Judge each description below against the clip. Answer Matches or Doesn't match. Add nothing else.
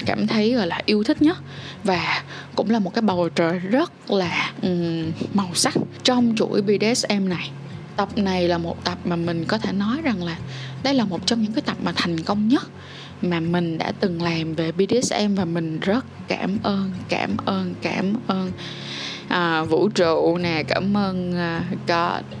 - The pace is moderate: Matches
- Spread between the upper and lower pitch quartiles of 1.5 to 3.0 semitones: Doesn't match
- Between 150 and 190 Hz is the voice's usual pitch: Matches